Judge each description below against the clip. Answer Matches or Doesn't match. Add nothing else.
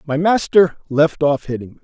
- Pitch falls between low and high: Matches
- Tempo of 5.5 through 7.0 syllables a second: Doesn't match